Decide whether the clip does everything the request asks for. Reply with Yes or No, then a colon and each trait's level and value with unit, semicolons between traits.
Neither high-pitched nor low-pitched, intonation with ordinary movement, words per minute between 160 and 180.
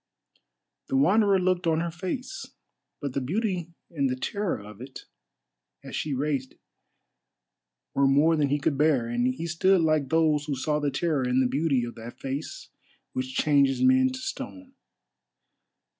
Yes: medium, 150 Hz; average, 4.5 semitones; average, 165 wpm